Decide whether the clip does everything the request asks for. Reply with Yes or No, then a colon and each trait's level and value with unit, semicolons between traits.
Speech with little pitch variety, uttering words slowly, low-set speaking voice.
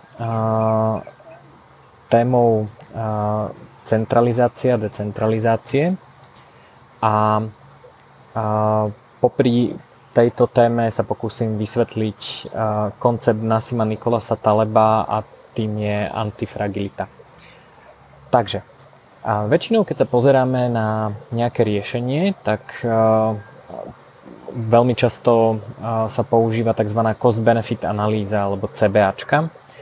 Yes: narrow, 2.0 semitones; slow, 70 wpm; low, 115 Hz